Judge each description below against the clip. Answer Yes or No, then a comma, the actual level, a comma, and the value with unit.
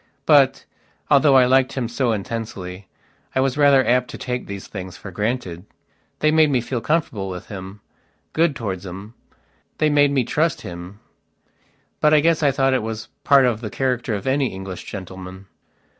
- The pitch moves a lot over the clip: Yes, wide, 5.9 semitones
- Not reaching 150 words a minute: No, average, 175 wpm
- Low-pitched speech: Yes, low, 120 Hz